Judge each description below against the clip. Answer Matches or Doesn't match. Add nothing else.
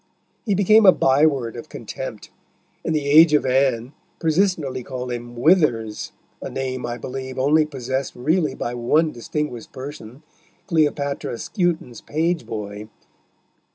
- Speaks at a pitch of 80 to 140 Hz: Matches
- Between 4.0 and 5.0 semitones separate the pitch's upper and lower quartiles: Matches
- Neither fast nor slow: Doesn't match